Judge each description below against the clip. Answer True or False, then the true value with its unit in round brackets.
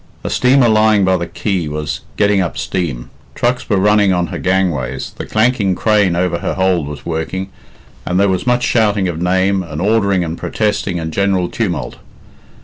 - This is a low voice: True (95 Hz)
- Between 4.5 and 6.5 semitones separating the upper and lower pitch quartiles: False (3.3 semitones)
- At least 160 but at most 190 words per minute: True (180 wpm)